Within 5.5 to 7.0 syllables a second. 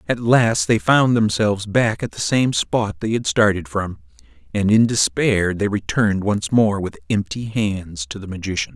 No: 4.6 syllables/s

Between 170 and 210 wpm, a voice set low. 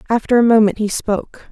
No: average, 200 wpm; high, 220 Hz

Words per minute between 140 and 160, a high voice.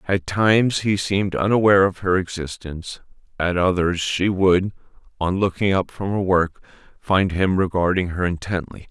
No: average, 155 wpm; very low, 95 Hz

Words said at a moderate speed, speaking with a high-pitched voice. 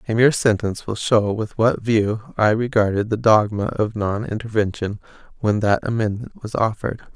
No: average, 170 wpm; low, 110 Hz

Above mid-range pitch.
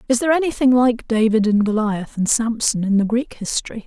Yes: high, 230 Hz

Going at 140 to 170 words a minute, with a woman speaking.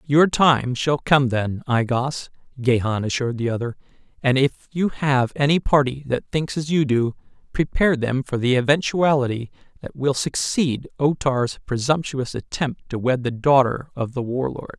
No: average, 165 wpm; male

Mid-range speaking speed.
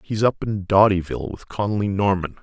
Yes: average, 175 wpm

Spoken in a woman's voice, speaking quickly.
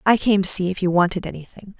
Yes: female; fast, 265 wpm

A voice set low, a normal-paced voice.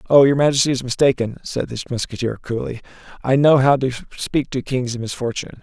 Yes: low, 130 Hz; average, 190 wpm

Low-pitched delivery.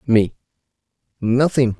Yes: low, 120 Hz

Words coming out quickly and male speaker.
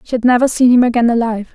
No: fast, 270 wpm; female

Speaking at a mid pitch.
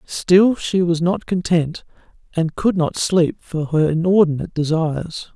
Yes: medium, 170 Hz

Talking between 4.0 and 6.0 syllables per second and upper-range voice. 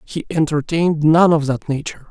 No: 5.6 syllables/s; medium, 155 Hz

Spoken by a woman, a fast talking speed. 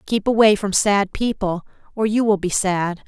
No: female; average, 195 wpm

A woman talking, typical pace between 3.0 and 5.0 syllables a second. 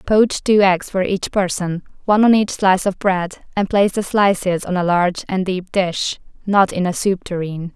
Yes: female; 4.5 syllables/s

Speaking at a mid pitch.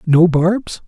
Yes: medium, 175 Hz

